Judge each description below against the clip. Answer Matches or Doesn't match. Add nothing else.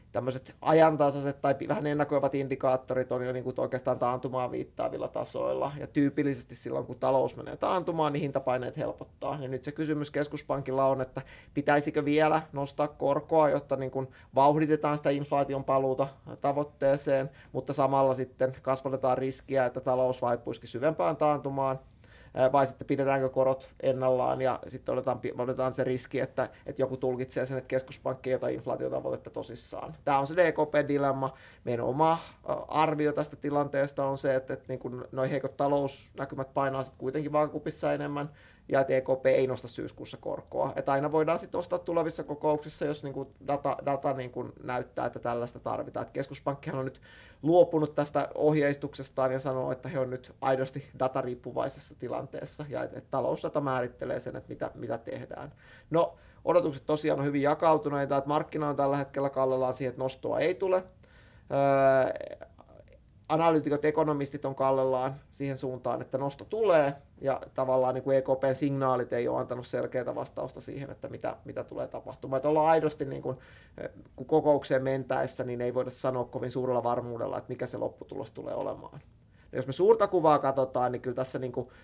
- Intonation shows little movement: Matches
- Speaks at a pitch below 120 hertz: Doesn't match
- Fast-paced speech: Matches